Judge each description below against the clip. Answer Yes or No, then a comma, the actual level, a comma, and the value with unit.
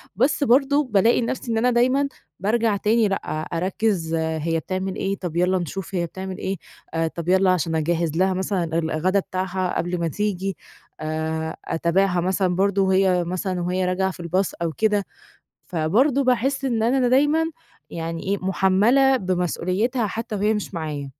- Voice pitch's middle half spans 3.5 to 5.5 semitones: Yes, average, 4.2 semitones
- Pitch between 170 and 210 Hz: Yes, high, 190 Hz